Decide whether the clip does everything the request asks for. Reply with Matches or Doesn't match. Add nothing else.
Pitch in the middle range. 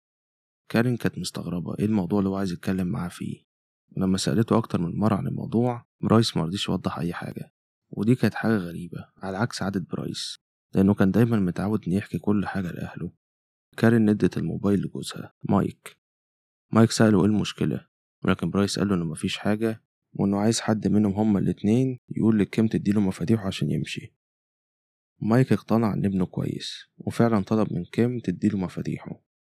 Doesn't match